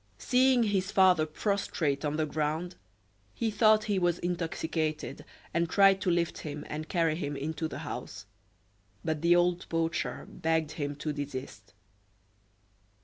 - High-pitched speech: No, medium, 165 Hz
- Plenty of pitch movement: No, average, 3.2 semitones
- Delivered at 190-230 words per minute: No, average, 145 wpm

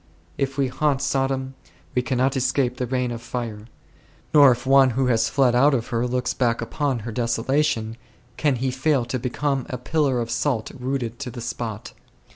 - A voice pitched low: Yes, low, 125 Hz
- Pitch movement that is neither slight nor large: No, narrow, 2.3 semitones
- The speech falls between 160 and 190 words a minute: Yes, average, 185 wpm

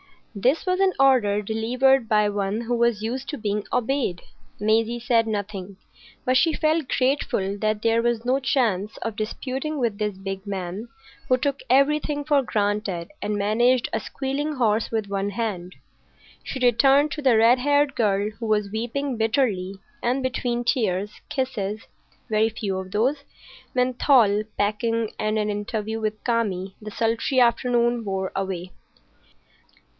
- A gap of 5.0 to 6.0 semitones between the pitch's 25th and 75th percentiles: No, average, 3.8 semitones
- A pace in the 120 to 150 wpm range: Yes, average, 145 wpm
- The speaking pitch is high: Yes, high, 225 Hz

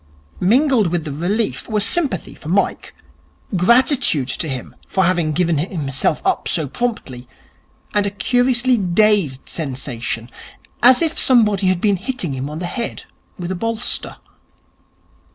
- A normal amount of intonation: No, wide, 7.2 semitones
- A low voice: No, medium, 185 Hz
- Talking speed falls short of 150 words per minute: Yes, average, 140 wpm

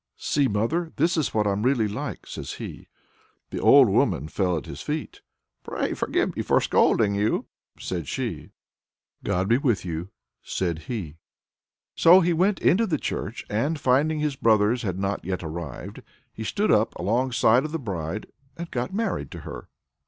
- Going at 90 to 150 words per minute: No, average, 170 wpm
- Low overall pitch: Yes, low, 110 Hz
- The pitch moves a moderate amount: No, wide, 8.1 semitones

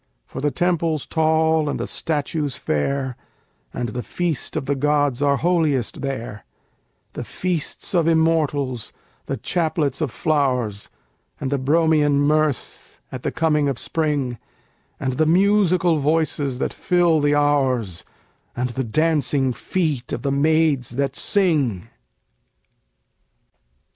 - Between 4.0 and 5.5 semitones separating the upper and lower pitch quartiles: No, average, 3.3 semitones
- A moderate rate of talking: No, slow, 130 wpm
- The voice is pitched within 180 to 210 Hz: No, medium, 145 Hz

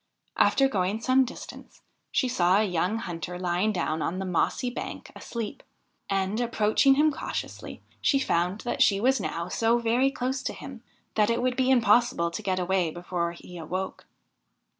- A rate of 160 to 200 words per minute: Yes, average, 170 wpm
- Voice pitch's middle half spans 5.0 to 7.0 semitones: Yes, wide, 5.5 semitones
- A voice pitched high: Yes, high, 210 Hz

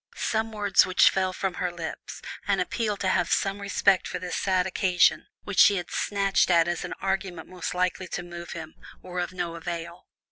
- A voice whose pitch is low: No, medium, 185 Hz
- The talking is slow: No, average, 200 wpm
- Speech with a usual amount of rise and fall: No, narrow, 2.0 semitones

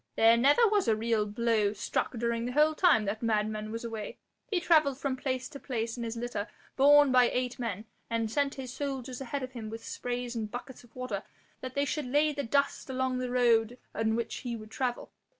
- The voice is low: No, high, 245 Hz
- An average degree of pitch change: Yes, average, 3.1 semitones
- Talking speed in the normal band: No, fast, 215 wpm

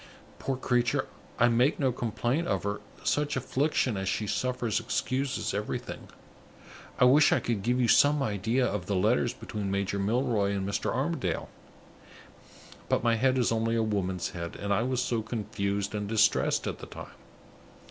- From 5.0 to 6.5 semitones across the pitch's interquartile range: No, average, 3.9 semitones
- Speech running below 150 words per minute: No, average, 170 wpm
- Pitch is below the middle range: Yes, low, 115 Hz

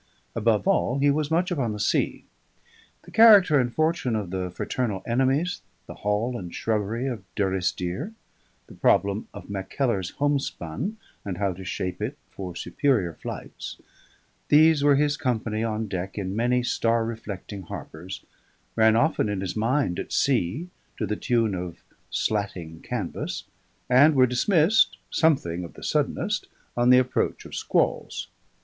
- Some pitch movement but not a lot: No, wide, 6.3 semitones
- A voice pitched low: Yes, low, 115 Hz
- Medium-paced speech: Yes, average, 150 wpm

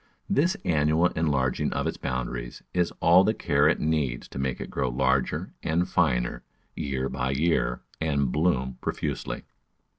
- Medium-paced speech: Yes, average, 150 wpm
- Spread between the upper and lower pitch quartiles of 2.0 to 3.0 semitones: No, average, 3.9 semitones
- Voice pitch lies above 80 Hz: No, very low, 70 Hz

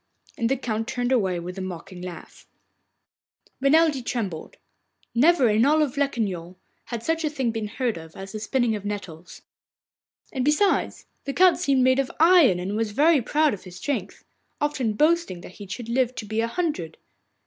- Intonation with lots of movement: Yes, wide, 6.4 semitones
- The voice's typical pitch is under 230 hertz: No, high, 235 Hz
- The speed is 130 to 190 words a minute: Yes, average, 180 wpm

